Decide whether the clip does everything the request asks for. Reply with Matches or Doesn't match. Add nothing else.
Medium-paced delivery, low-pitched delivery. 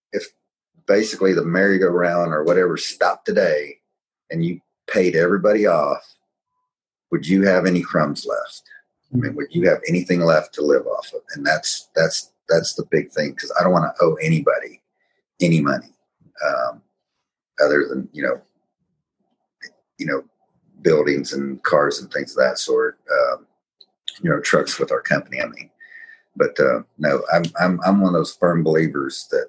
Matches